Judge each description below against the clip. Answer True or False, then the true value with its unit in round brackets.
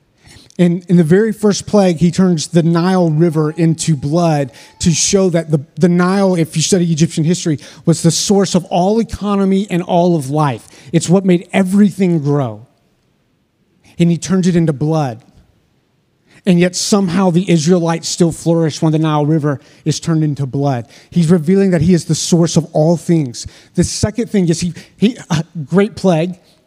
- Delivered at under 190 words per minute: True (180 wpm)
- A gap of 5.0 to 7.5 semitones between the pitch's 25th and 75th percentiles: False (2.7 semitones)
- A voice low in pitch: False (170 Hz)